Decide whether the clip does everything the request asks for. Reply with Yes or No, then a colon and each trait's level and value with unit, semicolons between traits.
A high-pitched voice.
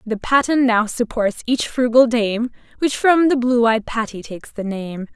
Yes: high, 235 Hz